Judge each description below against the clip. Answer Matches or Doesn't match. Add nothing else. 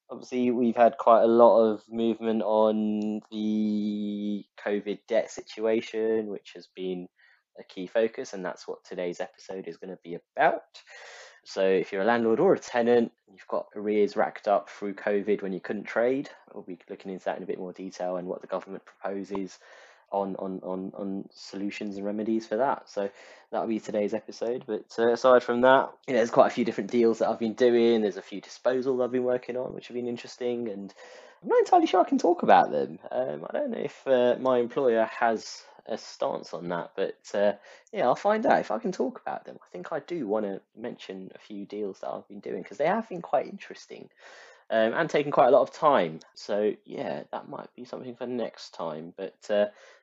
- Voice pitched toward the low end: Matches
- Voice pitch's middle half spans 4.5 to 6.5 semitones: Doesn't match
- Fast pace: Matches